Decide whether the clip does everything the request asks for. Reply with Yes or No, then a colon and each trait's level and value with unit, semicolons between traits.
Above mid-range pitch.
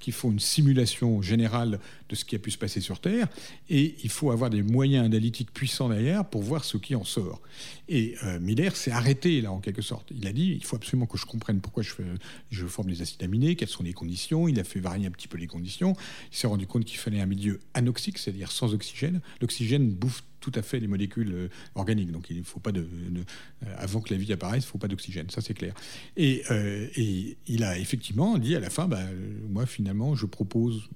No: low, 110 Hz